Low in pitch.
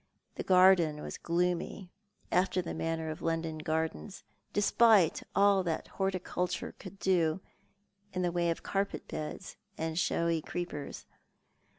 No: medium, 175 Hz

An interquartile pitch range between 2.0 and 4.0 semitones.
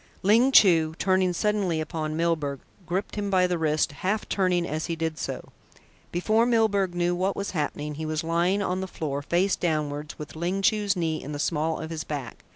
Yes: average, 3.5 semitones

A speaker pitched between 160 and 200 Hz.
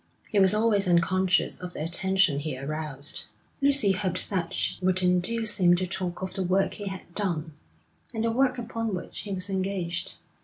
Yes: medium, 185 Hz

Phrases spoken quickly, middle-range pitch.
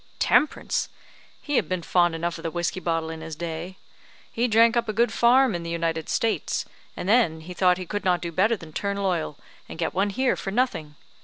Yes: fast, 220 wpm; medium, 180 Hz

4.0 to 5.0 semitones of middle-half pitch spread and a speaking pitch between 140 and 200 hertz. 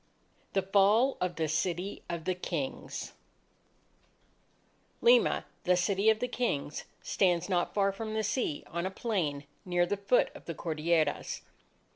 No: average, 3.3 semitones; medium, 185 Hz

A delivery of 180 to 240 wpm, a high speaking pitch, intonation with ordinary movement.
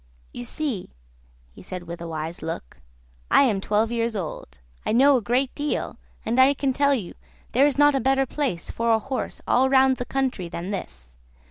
No: average, 200 wpm; high, 235 Hz; wide, 7.3 semitones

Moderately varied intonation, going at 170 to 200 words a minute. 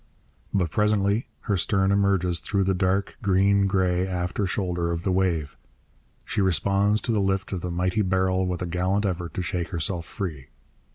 No: narrow, 1.9 semitones; average, 175 wpm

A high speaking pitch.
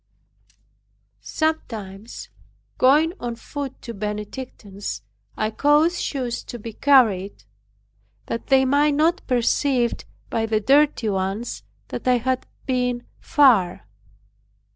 Yes: high, 245 Hz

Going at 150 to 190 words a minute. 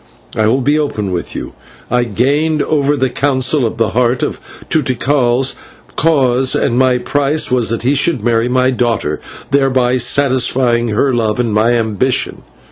Yes: average, 160 wpm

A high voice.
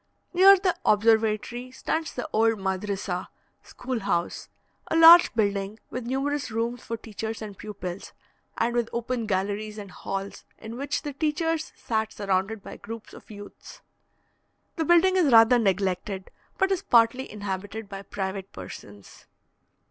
Yes: high, 220 Hz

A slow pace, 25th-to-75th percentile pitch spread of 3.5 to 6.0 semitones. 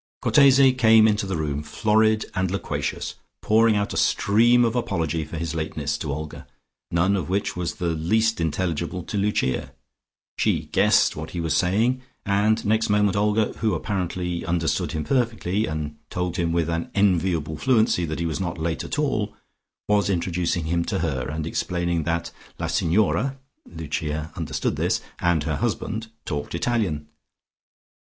No: average, 160 wpm; average, 4.7 semitones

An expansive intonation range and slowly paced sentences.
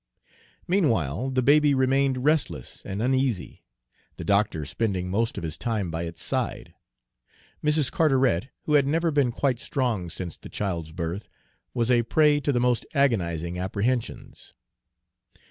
No: wide, 7.0 semitones; average, 145 wpm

